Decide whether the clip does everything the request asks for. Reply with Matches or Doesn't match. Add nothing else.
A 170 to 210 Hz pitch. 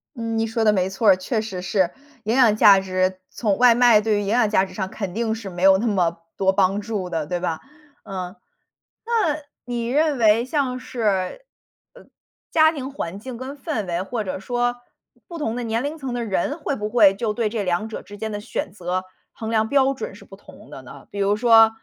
Doesn't match